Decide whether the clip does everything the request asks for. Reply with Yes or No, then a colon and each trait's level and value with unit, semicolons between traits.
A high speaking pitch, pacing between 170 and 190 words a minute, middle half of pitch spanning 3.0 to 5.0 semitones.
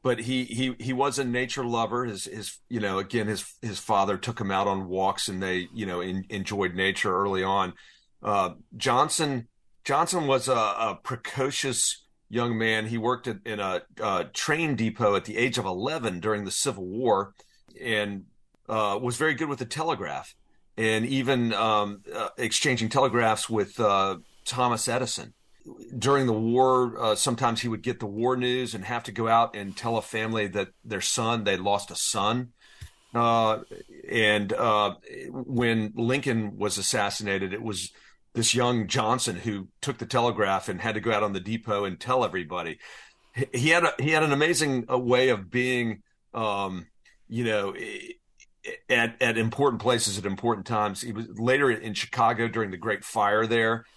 No: low, 115 Hz; average, 175 wpm; average, 3.5 semitones